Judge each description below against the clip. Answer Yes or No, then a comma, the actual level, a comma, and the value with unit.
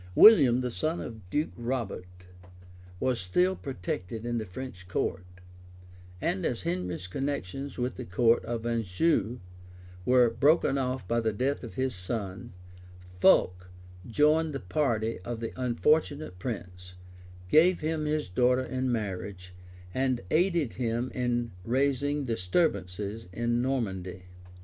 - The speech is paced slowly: Yes, slow, 130 wpm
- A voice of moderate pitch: No, low, 120 Hz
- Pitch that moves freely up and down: Yes, wide, 5.9 semitones